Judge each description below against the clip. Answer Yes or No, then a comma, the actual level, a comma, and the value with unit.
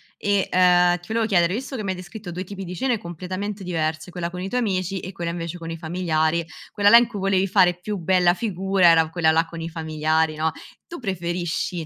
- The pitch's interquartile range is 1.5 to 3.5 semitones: Yes, average, 2.7 semitones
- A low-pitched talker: No, medium, 180 Hz